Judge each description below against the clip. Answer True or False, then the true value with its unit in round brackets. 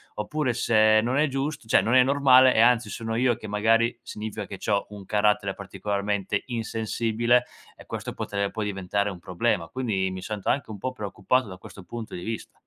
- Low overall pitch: True (110 Hz)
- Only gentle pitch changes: False (3.2 semitones)